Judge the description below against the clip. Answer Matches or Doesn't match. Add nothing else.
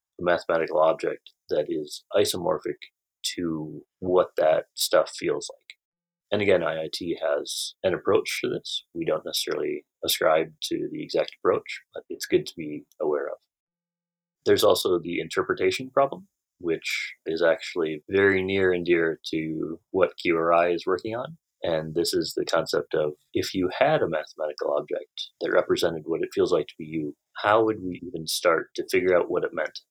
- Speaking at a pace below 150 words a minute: Doesn't match